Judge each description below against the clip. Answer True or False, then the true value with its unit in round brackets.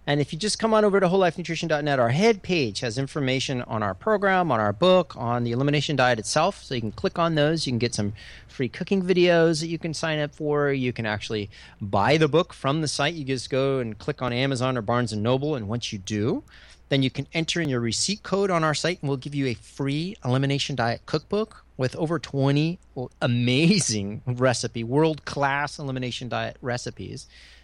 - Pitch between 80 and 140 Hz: True (135 Hz)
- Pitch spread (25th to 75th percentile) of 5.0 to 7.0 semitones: True (5.3 semitones)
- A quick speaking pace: True (210 wpm)